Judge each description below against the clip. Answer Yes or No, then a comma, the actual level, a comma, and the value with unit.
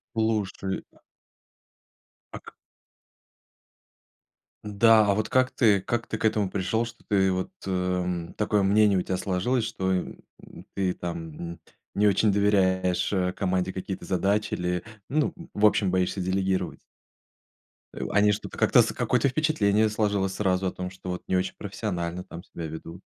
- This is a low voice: Yes, very low, 95 Hz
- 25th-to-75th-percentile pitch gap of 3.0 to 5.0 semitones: No, narrow, 2.5 semitones